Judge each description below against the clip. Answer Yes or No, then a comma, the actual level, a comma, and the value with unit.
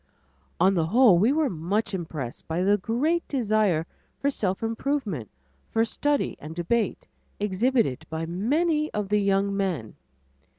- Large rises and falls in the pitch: Yes, wide, 5.8 semitones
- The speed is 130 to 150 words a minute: Yes, average, 140 wpm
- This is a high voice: Yes, high, 205 Hz